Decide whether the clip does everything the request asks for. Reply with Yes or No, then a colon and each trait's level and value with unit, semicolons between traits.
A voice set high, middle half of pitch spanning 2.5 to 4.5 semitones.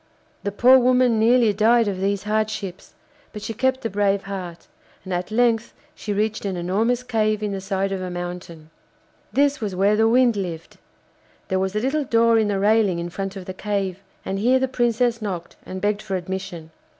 Yes: high, 205 Hz; average, 3.3 semitones